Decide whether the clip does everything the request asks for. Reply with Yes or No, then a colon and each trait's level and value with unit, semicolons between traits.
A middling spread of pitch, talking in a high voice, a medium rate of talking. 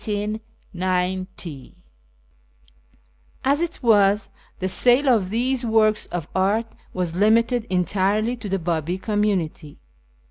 No: average, 3.7 semitones; high, 210 Hz; slow, 110 wpm